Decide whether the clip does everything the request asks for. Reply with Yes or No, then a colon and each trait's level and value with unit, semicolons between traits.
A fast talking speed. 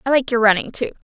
Yes: fast, 270 wpm